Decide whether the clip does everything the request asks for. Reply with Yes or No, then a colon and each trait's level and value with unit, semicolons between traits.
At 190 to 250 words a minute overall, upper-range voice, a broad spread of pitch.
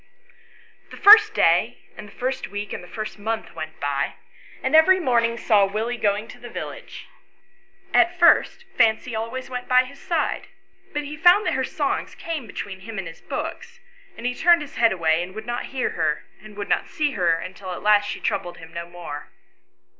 Yes: average, 200 wpm; high, 225 Hz; wide, 6.8 semitones